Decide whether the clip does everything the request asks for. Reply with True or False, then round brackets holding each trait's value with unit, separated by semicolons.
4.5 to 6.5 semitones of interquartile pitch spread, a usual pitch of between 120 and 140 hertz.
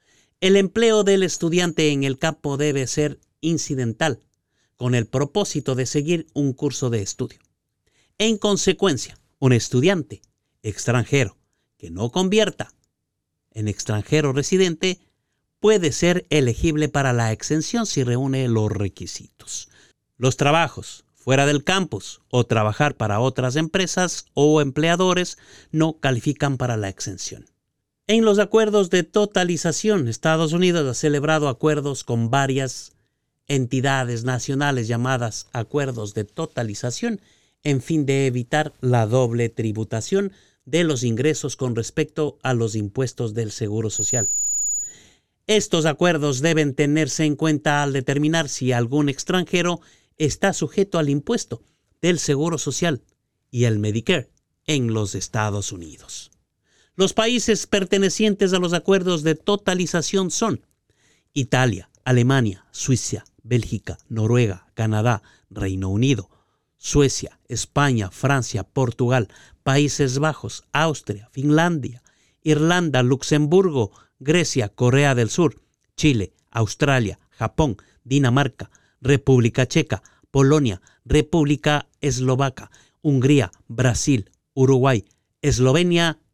True (5.4 semitones; 135 Hz)